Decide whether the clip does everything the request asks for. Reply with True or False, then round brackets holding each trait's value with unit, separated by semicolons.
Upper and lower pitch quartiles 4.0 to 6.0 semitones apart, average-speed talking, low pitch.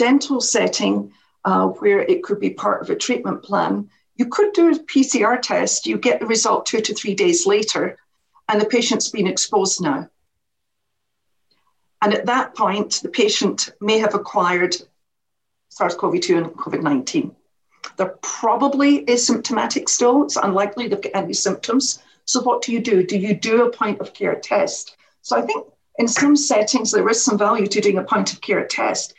False (5.2 semitones; 180 wpm; 240 Hz)